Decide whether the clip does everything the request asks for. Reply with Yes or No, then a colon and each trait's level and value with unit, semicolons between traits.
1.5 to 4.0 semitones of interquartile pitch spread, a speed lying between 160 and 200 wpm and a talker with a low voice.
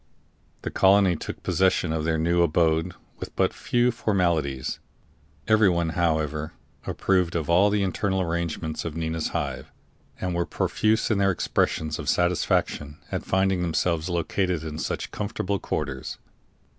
No: average, 3.2 semitones; average, 140 wpm; very low, 85 Hz